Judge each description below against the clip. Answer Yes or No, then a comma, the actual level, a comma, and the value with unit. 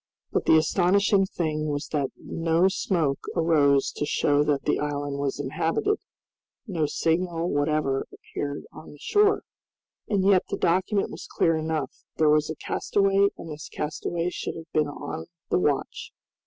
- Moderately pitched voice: Yes, medium, 160 Hz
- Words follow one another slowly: No, average, 155 wpm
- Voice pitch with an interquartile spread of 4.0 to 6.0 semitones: No, average, 3.5 semitones